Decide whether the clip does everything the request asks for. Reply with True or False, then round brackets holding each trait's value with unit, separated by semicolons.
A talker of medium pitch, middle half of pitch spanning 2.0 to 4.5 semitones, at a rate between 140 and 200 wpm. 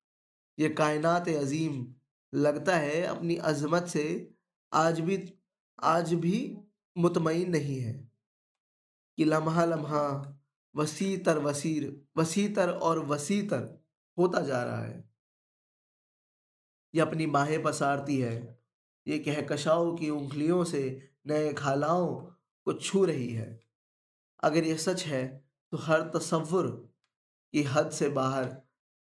False (155 Hz; 3.5 semitones; 115 wpm)